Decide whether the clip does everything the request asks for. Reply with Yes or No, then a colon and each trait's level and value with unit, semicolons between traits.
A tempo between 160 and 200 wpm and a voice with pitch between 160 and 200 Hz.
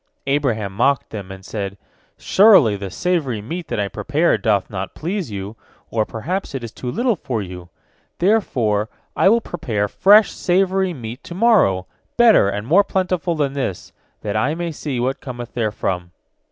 No: average, 165 wpm; low, 130 Hz